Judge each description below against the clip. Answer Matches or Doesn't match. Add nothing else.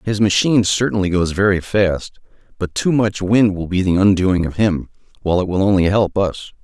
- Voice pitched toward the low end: Matches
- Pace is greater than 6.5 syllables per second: Doesn't match